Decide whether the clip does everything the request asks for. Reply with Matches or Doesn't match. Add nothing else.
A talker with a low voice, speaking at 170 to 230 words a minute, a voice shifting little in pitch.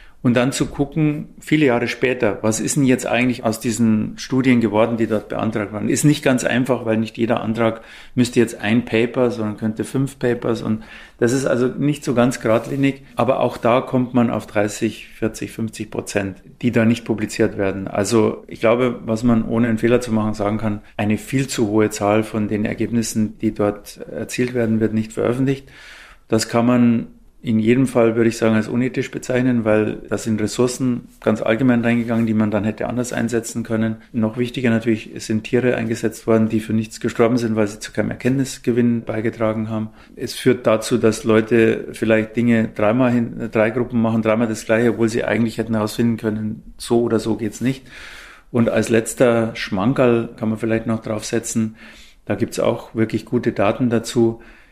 Matches